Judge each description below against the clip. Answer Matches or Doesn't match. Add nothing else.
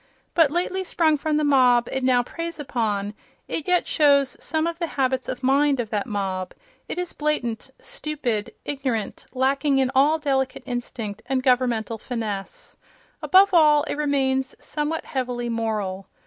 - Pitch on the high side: Matches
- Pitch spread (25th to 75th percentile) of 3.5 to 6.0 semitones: Matches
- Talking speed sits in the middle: Matches